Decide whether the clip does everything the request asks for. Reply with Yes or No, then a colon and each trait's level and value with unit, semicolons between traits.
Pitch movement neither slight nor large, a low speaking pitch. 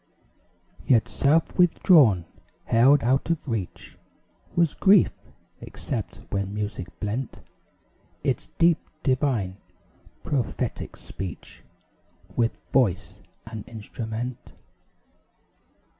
No: wide, 5.7 semitones; low, 120 Hz